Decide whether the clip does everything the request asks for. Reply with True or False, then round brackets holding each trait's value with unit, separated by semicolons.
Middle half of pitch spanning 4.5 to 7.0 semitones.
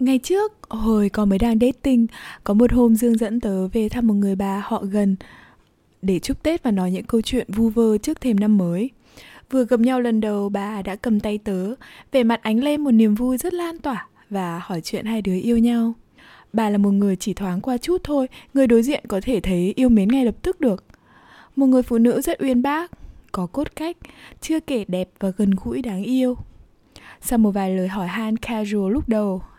False (4.0 semitones)